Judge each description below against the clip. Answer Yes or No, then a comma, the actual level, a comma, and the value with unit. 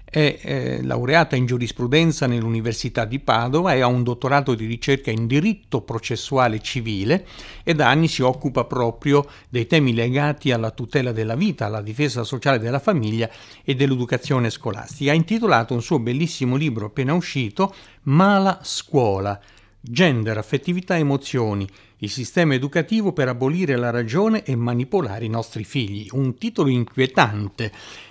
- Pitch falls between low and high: No, low, 130 Hz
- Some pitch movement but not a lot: Yes, average, 4.3 semitones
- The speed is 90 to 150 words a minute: Yes, average, 145 wpm